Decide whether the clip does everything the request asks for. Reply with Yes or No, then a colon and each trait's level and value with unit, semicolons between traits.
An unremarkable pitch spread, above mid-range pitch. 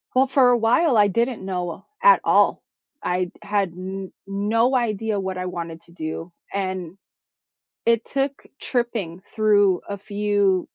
Yes: average, 4.0 semitones; high, 200 Hz